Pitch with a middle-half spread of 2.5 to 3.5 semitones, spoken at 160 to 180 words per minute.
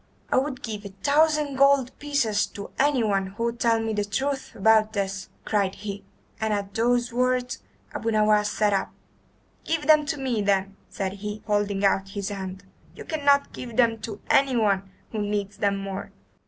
No: average, 4.1 semitones; average, 175 wpm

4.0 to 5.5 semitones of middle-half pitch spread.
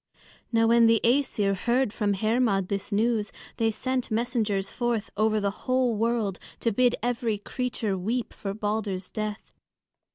No: average, 2.8 semitones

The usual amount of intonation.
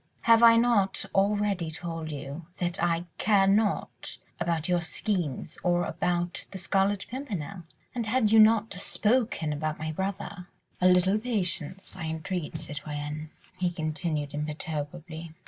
Yes: average, 4.4 semitones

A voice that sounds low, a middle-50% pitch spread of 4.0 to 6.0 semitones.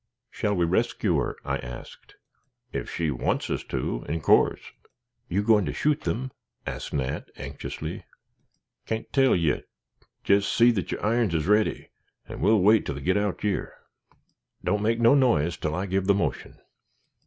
Yes: low, 100 Hz; average, 5.3 semitones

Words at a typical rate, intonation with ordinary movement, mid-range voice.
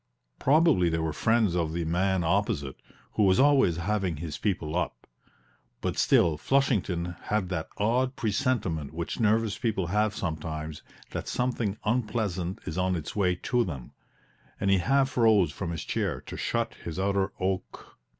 No: average, 160 wpm; average, 4.7 semitones; very low, 95 Hz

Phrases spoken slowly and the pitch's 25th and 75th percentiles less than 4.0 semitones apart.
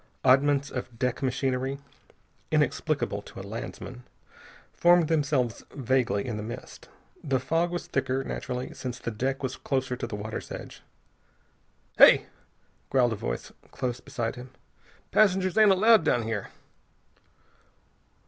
Yes: slow, 130 wpm; average, 2.8 semitones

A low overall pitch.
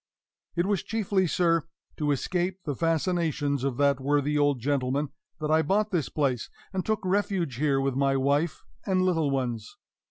No: medium, 150 Hz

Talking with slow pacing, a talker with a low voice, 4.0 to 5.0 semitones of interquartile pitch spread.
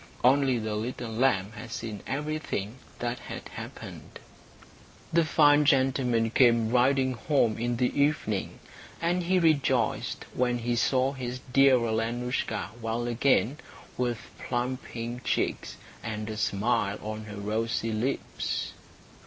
No: slow, 130 wpm; low, 120 Hz; average, 3.0 semitones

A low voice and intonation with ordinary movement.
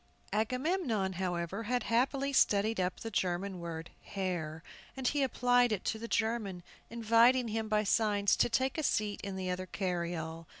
No: high, 210 Hz; average, 4.5 semitones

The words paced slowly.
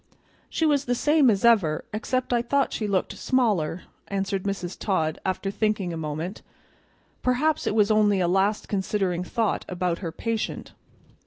No: average, 160 wpm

